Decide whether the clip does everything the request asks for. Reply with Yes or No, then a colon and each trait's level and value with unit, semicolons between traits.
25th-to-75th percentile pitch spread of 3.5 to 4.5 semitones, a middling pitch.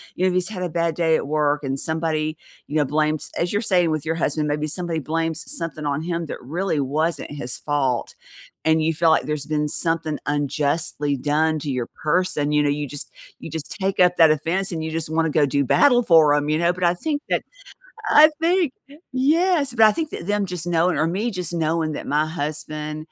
No: average, 2.9 semitones; medium, 160 Hz